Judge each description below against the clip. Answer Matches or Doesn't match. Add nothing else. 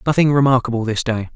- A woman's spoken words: Doesn't match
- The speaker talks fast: Doesn't match